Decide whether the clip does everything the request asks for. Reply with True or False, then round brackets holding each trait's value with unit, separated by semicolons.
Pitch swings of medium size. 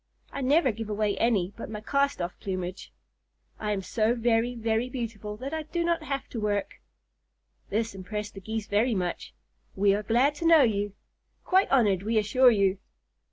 True (3.8 semitones)